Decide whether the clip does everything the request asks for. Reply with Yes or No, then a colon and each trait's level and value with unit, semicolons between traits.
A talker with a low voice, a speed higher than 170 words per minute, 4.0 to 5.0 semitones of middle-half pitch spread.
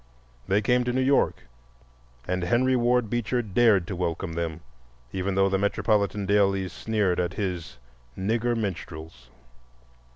No: low, 100 Hz; slow, 135 wpm; average, 4.4 semitones